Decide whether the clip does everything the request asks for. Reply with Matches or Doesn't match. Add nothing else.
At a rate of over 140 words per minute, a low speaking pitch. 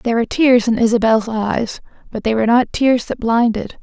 Doesn't match